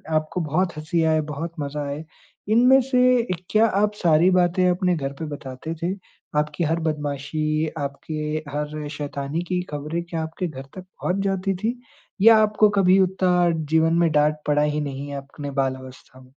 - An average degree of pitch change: Yes, average, 3.7 semitones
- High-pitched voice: No, medium, 160 Hz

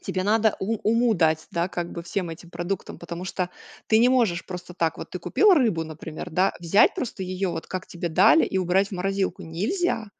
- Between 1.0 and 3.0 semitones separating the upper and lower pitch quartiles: No, average, 4.0 semitones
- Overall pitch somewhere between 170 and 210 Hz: Yes, medium, 185 Hz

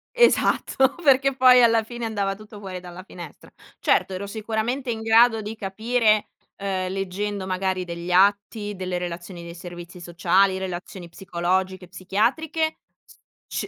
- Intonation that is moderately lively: Yes, average, 3.5 semitones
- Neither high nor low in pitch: No, high, 195 Hz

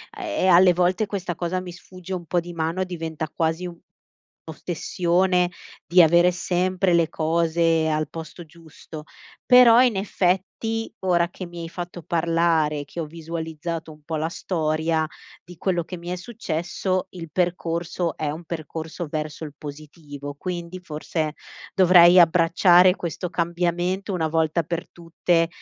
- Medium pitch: Yes, medium, 170 Hz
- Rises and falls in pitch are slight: Yes, narrow, 2.0 semitones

